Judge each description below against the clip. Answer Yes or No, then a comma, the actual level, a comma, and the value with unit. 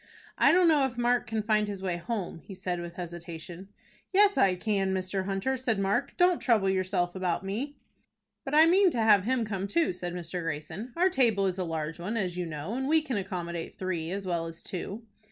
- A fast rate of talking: Yes, fast, 215 wpm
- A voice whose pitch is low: No, high, 195 Hz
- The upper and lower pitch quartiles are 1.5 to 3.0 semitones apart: No, average, 5.3 semitones